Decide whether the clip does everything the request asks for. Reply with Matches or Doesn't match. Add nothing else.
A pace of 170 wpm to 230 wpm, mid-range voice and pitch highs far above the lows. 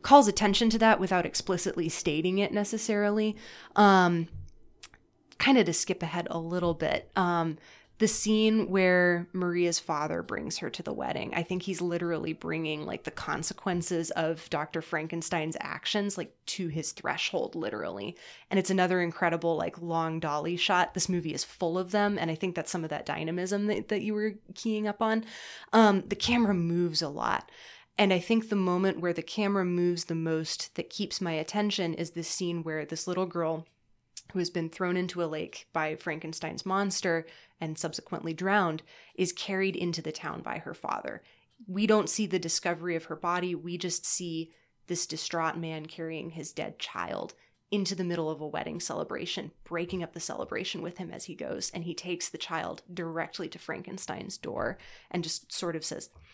Doesn't match